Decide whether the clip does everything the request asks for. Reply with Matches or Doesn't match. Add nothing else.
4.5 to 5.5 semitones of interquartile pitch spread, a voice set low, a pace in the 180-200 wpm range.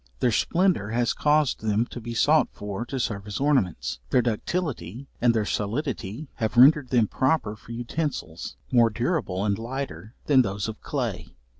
Doesn't match